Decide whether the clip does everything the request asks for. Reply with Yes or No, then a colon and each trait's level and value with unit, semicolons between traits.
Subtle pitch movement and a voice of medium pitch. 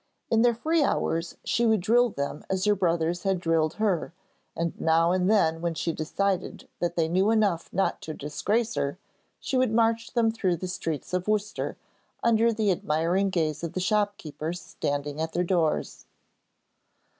No: average, 4.7 semitones; medium, 180 Hz